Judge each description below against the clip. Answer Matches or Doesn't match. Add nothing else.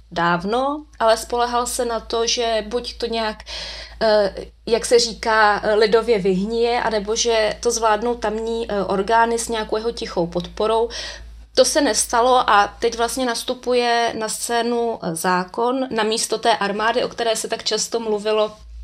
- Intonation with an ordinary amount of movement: Doesn't match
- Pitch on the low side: Doesn't match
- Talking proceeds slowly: Doesn't match